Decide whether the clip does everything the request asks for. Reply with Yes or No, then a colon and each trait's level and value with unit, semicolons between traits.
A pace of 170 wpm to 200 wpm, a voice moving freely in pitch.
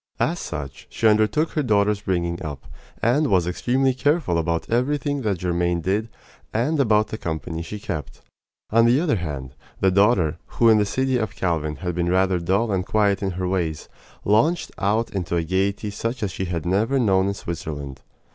No: average, 185 wpm; average, 4.9 semitones